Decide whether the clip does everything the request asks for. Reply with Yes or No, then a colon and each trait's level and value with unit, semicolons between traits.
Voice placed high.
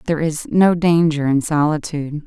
No: medium, 155 Hz